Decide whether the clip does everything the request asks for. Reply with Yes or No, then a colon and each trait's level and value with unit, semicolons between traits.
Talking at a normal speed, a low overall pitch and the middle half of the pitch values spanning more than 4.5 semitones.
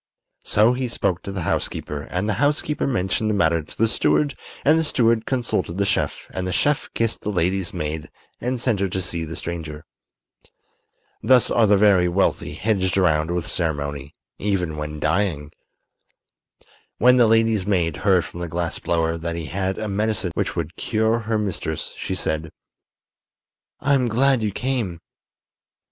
Yes: average, 165 wpm; very low, 95 Hz; average, 5.1 semitones